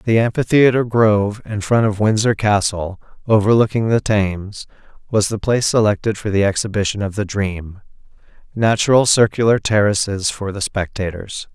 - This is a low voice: Yes, low, 105 Hz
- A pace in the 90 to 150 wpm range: Yes, average, 140 wpm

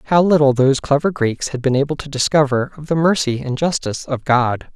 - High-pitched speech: No, medium, 140 Hz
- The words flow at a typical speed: No, fast, 215 wpm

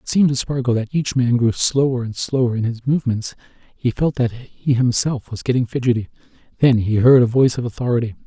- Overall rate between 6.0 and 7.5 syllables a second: Yes, 6.1 syllables/s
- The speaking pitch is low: Yes, low, 125 Hz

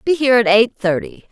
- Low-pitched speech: No, high, 235 Hz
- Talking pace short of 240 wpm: Yes, fast, 230 wpm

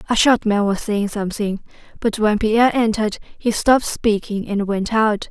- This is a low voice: No, high, 215 Hz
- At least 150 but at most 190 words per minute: Yes, average, 180 wpm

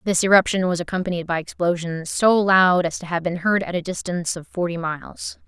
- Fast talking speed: Yes, fast, 210 wpm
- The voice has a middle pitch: Yes, medium, 175 Hz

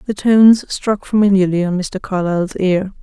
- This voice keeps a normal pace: Yes, average, 160 wpm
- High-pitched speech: Yes, high, 195 Hz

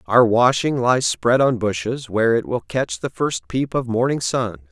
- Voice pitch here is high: No, low, 120 Hz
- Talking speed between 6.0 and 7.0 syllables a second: No, 4.5 syllables/s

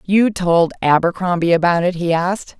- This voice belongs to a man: No, female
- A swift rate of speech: No, average, 160 wpm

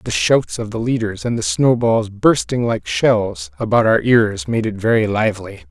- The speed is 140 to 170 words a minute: No, average, 190 wpm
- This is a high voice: No, low, 115 Hz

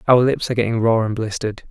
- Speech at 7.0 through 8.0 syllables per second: Yes, 7.1 syllables/s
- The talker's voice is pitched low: Yes, low, 115 Hz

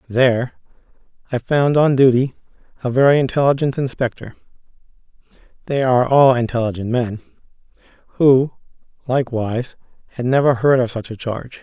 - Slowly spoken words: Yes, slow, 120 wpm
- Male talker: Yes, male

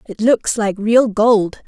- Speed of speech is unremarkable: Yes, average, 180 wpm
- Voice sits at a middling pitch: No, high, 215 Hz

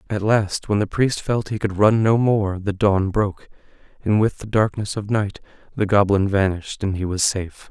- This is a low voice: Yes, low, 100 Hz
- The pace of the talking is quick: Yes, fast, 210 wpm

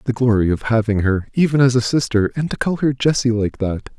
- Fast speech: Yes, fast, 240 wpm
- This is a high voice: No, low, 120 Hz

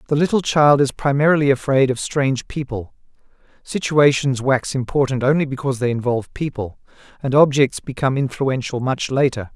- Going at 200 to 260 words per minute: No, average, 145 wpm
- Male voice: Yes, male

